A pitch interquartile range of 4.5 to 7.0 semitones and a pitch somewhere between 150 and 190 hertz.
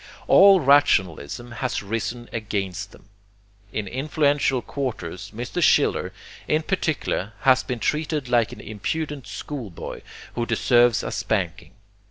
No: wide, 5.4 semitones; low, 120 Hz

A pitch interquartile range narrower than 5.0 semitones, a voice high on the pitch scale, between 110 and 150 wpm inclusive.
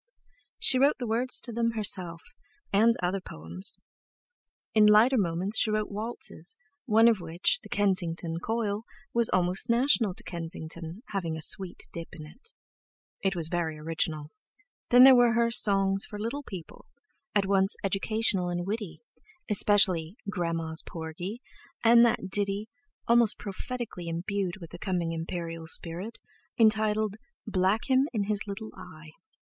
Yes: average, 4.6 semitones; high, 195 Hz; average, 145 wpm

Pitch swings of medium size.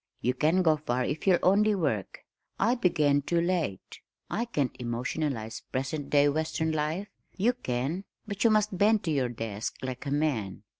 No: wide, 6.5 semitones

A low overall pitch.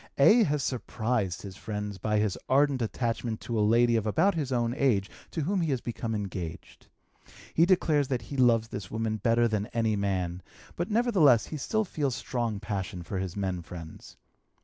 Yes: low, 115 Hz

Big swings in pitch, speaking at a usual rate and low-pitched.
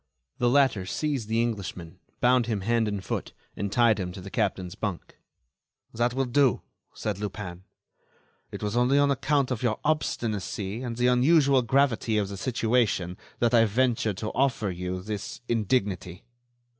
No: average, 4.0 semitones; average, 160 wpm; low, 115 Hz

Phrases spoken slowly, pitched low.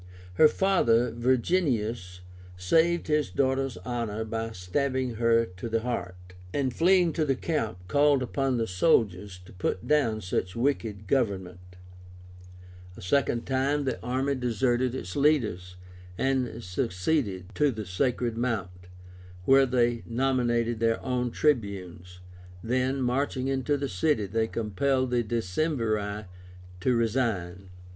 Yes: slow, 125 wpm; low, 120 Hz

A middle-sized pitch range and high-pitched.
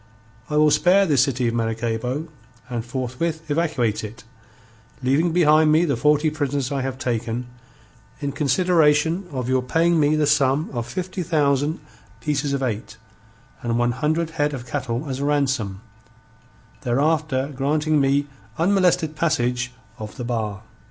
No: average, 3.9 semitones; medium, 140 Hz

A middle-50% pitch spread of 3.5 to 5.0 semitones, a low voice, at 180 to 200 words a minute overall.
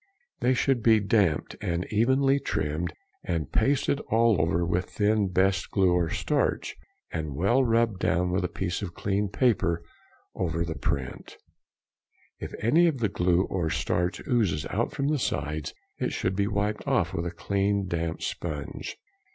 No: average, 4.7 semitones; very low, 95 Hz; average, 165 wpm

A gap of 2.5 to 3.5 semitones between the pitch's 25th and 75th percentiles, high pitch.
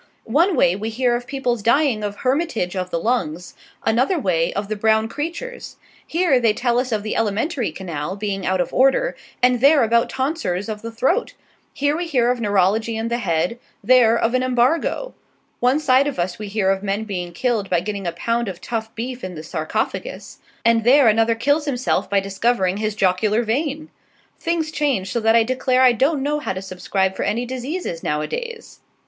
No: average, 5.0 semitones; high, 230 Hz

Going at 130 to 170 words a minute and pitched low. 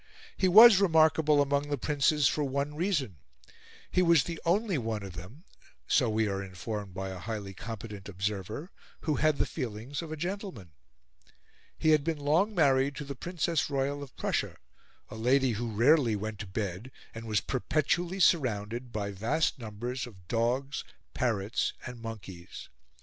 Yes: average, 160 wpm; low, 130 Hz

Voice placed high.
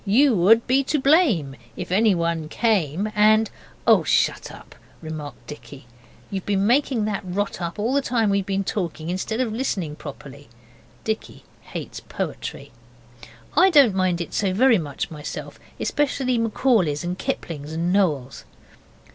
Yes: high, 195 Hz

